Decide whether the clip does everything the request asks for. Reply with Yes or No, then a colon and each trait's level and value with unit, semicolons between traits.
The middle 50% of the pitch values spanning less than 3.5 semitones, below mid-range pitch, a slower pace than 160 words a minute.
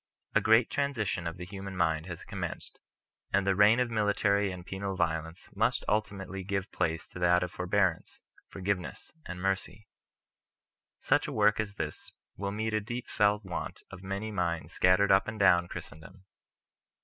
No: average, 2.7 semitones; very low, 95 Hz; average, 165 wpm